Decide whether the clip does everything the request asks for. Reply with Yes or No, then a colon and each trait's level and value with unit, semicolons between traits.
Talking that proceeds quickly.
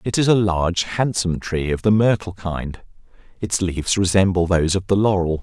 No: average, 190 wpm